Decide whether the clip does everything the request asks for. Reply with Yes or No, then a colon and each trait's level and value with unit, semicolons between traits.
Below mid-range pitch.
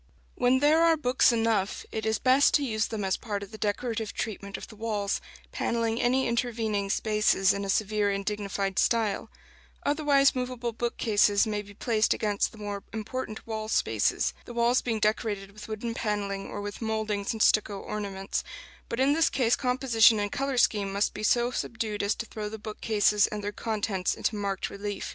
No: high, 215 Hz